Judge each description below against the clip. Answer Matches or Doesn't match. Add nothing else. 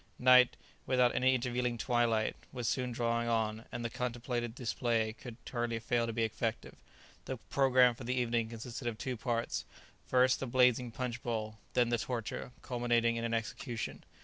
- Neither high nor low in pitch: Doesn't match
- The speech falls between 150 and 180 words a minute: Matches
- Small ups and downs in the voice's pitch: Matches